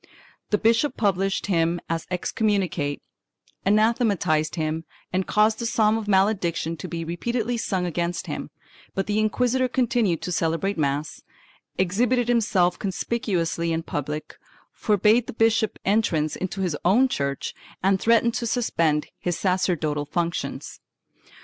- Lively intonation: No, average, 5.0 semitones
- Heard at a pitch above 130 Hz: Yes, high, 190 Hz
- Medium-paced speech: No, slow, 130 wpm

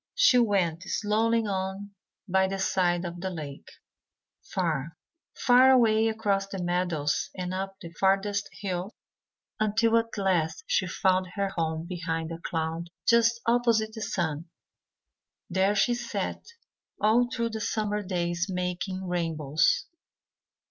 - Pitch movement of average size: Yes, average, 4.0 semitones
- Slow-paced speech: Yes, slow, 130 wpm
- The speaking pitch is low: No, high, 190 Hz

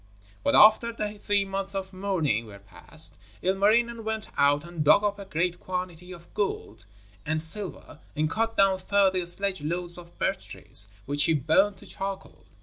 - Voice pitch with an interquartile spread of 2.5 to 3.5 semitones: No, average, 3.9 semitones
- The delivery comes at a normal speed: Yes, average, 170 wpm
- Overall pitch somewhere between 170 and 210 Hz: Yes, medium, 185 Hz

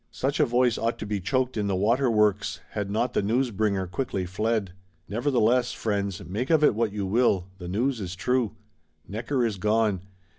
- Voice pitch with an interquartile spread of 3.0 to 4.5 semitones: Yes, average, 3.7 semitones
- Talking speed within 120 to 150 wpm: No, average, 185 wpm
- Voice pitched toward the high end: No, low, 110 Hz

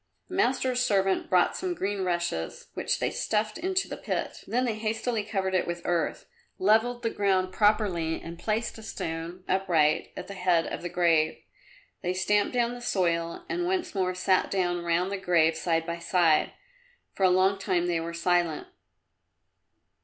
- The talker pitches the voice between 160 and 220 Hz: Yes, medium, 185 Hz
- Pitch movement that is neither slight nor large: Yes, average, 3.9 semitones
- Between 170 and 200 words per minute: Yes, average, 175 wpm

